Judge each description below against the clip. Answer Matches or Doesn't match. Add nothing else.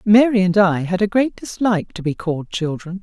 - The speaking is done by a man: Doesn't match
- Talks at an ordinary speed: Doesn't match